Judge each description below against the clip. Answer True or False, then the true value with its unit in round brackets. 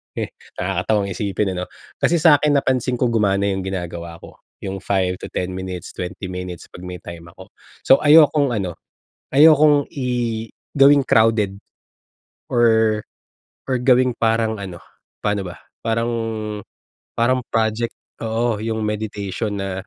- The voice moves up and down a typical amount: True (4.6 semitones)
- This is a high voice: False (110 Hz)